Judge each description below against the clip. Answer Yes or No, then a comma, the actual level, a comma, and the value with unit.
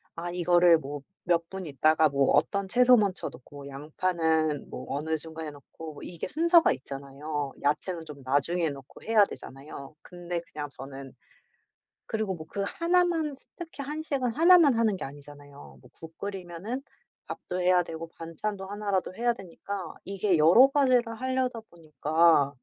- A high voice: No, medium, 175 Hz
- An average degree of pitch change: No, wide, 6.4 semitones